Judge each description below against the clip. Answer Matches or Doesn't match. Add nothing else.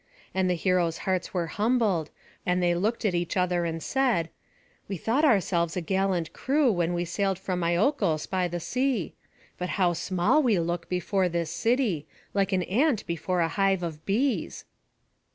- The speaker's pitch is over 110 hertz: Matches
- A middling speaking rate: Matches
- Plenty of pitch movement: Doesn't match